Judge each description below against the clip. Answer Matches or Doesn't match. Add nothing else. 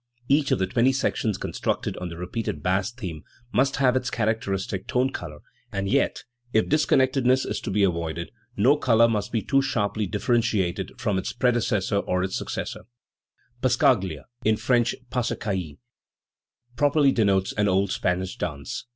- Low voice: Matches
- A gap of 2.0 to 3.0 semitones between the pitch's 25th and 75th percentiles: Doesn't match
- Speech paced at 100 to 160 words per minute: Matches